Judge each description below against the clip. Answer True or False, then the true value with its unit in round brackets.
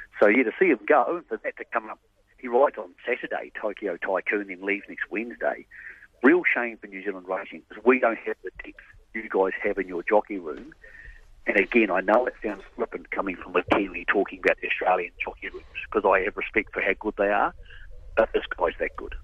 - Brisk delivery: True (220 wpm)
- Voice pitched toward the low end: False (390 Hz)